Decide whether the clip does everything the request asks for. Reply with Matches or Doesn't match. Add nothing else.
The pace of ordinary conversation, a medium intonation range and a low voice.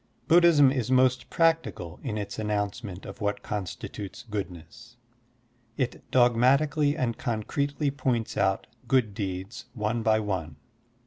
Doesn't match